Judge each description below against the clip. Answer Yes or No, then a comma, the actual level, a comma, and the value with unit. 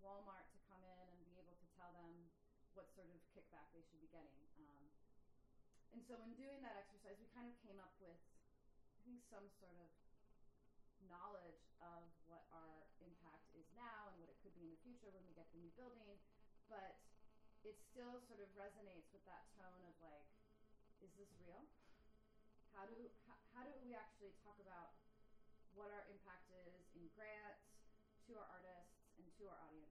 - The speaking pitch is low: No, high, 190 Hz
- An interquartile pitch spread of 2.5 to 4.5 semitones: Yes, average, 3.6 semitones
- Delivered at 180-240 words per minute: Yes, average, 185 wpm